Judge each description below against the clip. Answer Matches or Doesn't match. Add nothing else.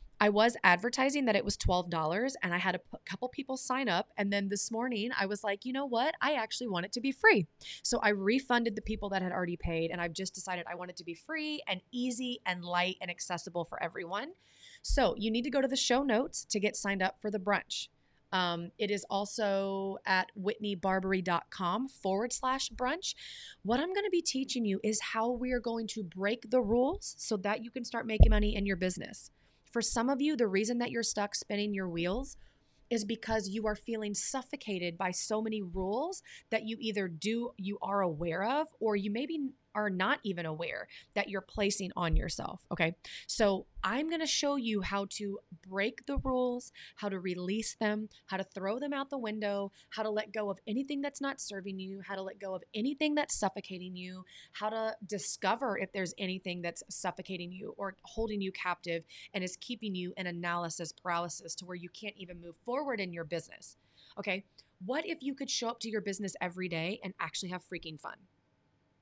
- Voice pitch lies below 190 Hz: Doesn't match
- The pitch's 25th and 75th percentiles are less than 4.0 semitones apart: Doesn't match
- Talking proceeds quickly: Matches